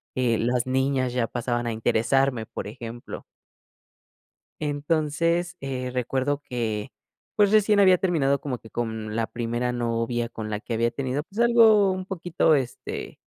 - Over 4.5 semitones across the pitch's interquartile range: Yes, average, 5.1 semitones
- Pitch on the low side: Yes, low, 130 Hz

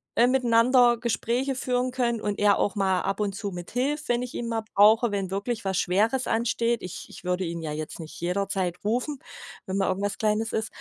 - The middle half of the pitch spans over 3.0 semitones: Yes, average, 3.8 semitones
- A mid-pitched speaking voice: No, high, 215 Hz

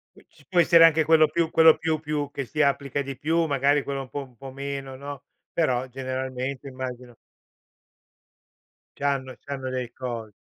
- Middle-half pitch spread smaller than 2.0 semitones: No, narrow, 2.6 semitones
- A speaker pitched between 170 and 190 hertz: No, medium, 140 Hz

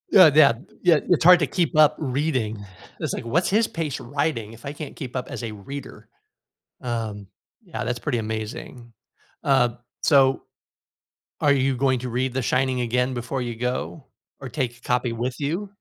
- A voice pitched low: Yes, low, 130 Hz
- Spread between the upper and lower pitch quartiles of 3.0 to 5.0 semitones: Yes, average, 3.6 semitones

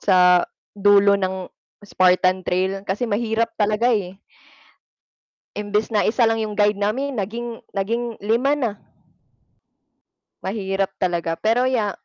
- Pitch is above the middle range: Yes, high, 205 Hz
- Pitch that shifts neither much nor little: Yes, average, 3.0 semitones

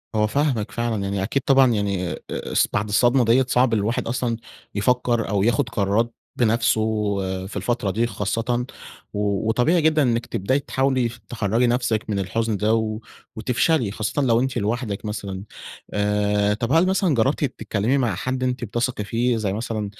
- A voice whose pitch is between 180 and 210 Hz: No, low, 115 Hz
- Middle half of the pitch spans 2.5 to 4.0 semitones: Yes, average, 3.2 semitones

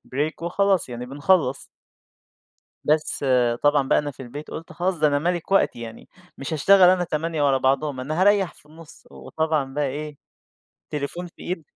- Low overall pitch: No, medium, 150 Hz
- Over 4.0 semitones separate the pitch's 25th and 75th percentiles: No, average, 3.7 semitones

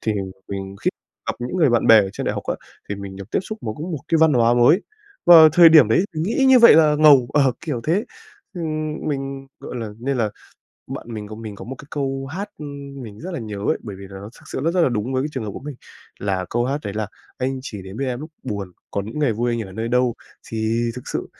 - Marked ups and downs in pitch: Yes, wide, 5.9 semitones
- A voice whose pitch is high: No, low, 125 Hz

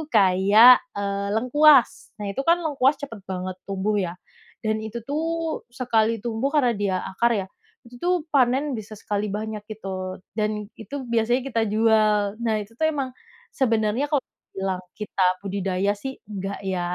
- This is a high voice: Yes, high, 220 Hz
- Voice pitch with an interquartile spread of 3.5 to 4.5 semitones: Yes, average, 3.9 semitones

